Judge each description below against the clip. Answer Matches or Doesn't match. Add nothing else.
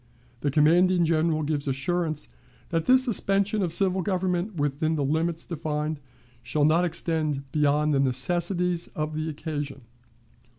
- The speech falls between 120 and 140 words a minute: Matches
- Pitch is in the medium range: Matches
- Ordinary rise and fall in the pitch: Matches